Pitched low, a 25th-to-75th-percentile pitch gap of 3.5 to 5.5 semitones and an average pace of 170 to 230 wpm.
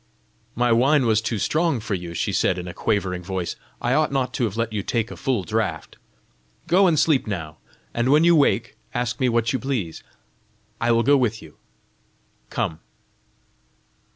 Yes: low, 115 Hz; average, 5.1 semitones; average, 180 wpm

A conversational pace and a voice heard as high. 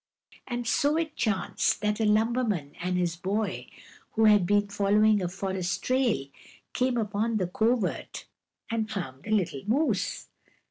Yes: average, 145 wpm; high, 210 Hz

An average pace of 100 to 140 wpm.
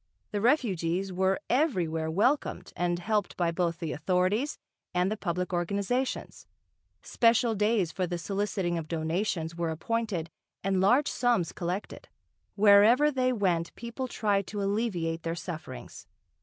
Yes: slow, 135 wpm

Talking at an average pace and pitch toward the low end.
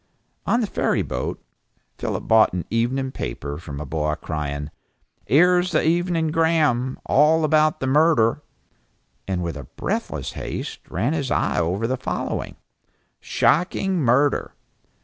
No: slow, 130 wpm; low, 130 Hz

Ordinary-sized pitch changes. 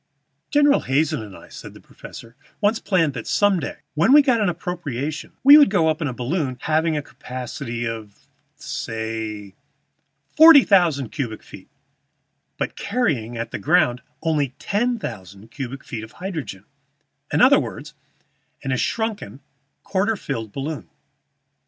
No: wide, 8.5 semitones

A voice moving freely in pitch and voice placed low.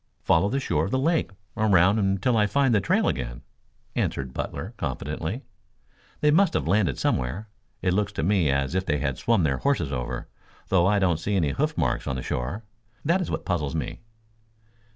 Yes: wide, 6.8 semitones; very low, 95 Hz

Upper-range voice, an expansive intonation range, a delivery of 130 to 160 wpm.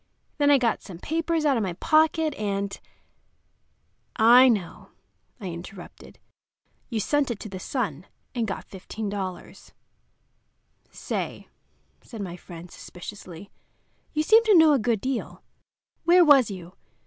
Yes: high, 220 Hz; wide, 7.3 semitones; slow, 135 wpm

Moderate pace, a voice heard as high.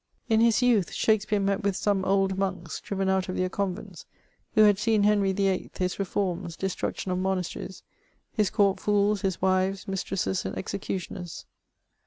Yes: average, 165 wpm; high, 195 Hz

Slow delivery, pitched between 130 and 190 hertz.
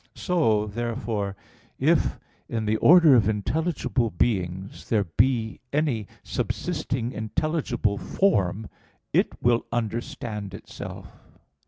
No: slow, 100 wpm; low, 115 Hz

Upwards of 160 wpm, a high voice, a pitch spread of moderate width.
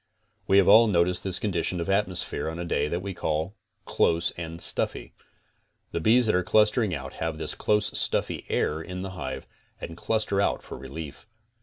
No: average, 185 wpm; very low, 90 Hz; average, 3.5 semitones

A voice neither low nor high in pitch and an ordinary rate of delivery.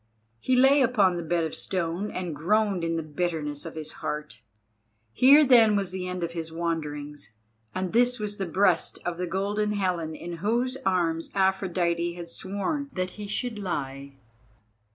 Yes: medium, 180 Hz; average, 170 wpm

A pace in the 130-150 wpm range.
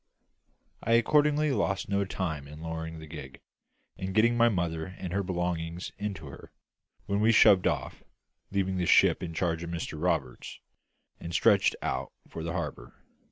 No: average, 160 wpm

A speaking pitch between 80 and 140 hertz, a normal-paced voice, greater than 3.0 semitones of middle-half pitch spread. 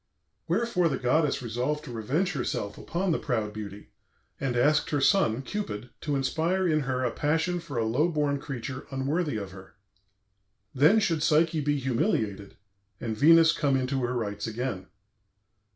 Yes: low, 135 Hz; average, 160 wpm; average, 5.0 semitones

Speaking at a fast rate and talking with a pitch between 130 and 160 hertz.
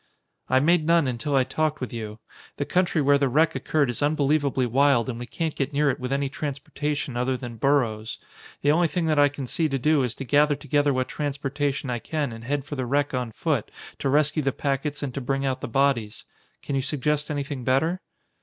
Yes: fast, 220 wpm; medium, 140 Hz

